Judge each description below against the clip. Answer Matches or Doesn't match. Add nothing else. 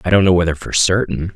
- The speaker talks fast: Matches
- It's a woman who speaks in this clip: Doesn't match